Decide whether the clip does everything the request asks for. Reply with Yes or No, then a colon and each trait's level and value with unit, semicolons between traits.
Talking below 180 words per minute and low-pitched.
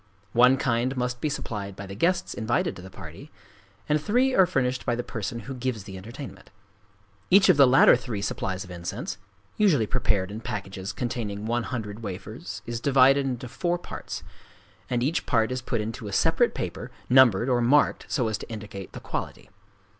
No: average, 185 wpm; low, 120 Hz